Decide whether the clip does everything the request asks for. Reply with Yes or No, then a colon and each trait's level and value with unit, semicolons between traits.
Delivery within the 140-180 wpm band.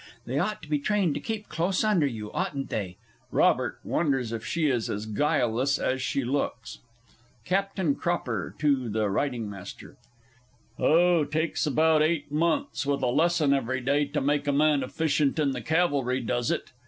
Yes: average, 170 wpm